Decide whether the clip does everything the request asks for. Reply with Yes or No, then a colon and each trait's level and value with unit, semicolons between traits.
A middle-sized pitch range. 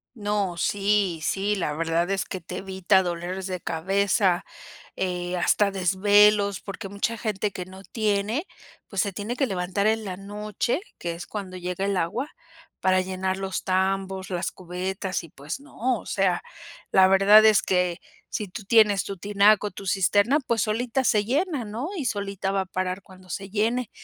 No: narrow, 2.2 semitones